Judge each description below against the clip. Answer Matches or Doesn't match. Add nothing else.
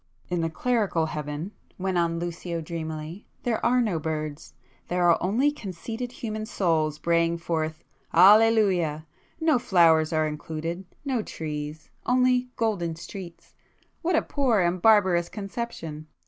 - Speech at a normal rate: Doesn't match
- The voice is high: Doesn't match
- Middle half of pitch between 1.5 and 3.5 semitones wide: Doesn't match